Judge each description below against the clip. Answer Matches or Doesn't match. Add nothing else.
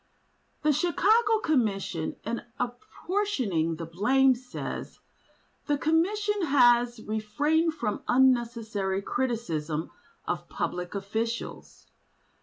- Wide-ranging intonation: Matches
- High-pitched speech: Matches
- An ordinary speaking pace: Doesn't match